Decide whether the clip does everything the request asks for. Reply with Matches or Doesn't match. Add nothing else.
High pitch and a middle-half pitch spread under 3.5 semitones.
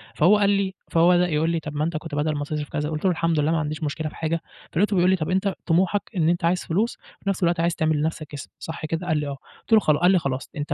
Doesn't match